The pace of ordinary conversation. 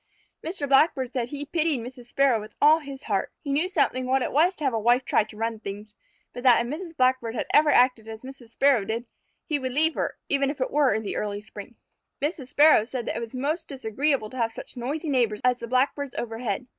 No: fast, 230 wpm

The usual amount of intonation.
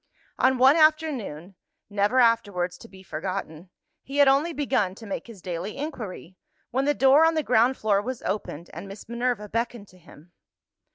No: wide, 5.9 semitones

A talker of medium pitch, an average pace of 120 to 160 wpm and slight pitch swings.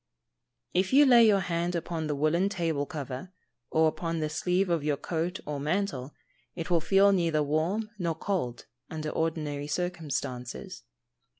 No: medium, 165 Hz; average, 155 wpm; average, 3.3 semitones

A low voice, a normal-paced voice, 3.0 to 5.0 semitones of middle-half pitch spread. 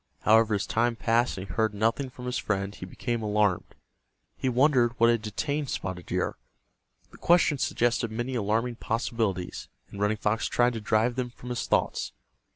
No: low, 115 Hz; average, 175 wpm; narrow, 2.6 semitones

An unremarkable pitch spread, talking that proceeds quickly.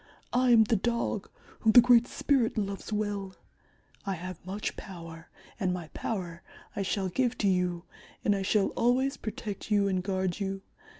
No: average, 3.4 semitones; average, 170 wpm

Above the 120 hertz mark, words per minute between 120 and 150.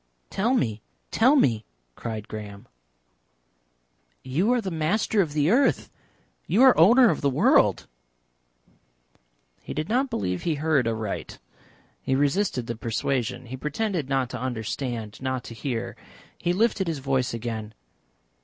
Yes: low, 135 Hz; average, 140 wpm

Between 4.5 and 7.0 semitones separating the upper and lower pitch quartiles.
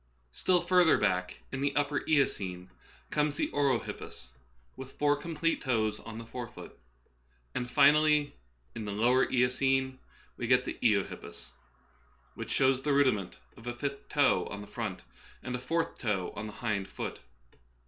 Yes: average, 4.9 semitones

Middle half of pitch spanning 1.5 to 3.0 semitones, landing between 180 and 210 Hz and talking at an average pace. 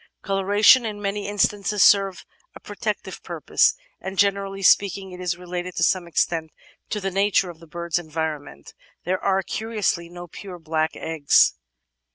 Yes: average, 2.7 semitones; medium, 185 Hz; average, 155 wpm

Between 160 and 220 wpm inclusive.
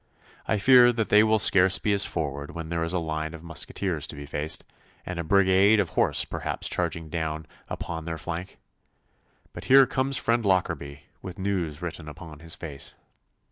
Yes: average, 180 wpm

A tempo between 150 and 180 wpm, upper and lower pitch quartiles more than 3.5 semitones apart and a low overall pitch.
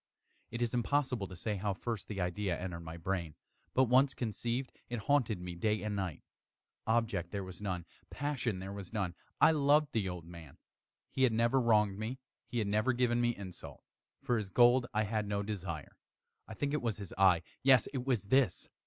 No: average, 195 wpm; average, 4.3 semitones; low, 105 Hz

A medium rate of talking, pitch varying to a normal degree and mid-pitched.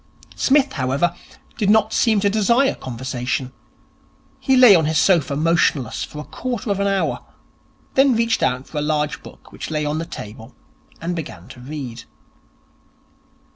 No: average, 160 wpm; wide, 7.9 semitones; medium, 160 Hz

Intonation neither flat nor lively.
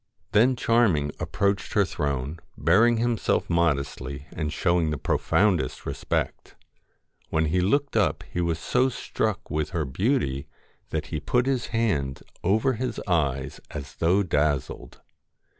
No: wide, 7.2 semitones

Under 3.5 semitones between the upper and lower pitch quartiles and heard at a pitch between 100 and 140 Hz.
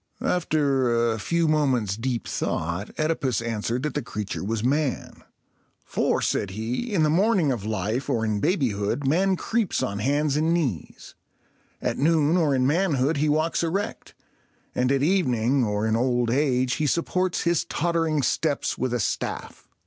No: wide, 5.4 semitones; low, 135 Hz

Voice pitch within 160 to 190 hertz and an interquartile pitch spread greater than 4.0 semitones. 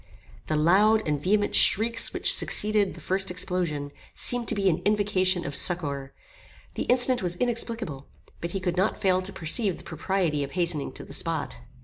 Yes: medium, 185 Hz; average, 4.6 semitones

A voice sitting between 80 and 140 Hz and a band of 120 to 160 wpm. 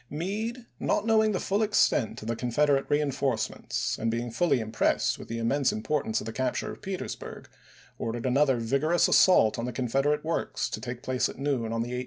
No: low, 135 Hz; average, 200 wpm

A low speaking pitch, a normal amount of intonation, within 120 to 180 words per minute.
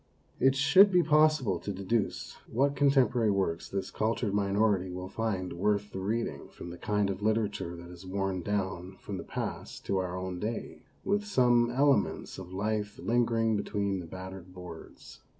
Yes: low, 105 Hz; average, 4.2 semitones; average, 175 wpm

